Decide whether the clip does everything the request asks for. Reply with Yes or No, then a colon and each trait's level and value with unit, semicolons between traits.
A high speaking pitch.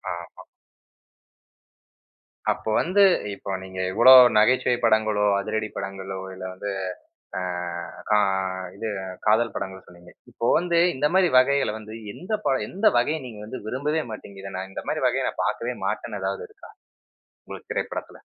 No: low, 110 Hz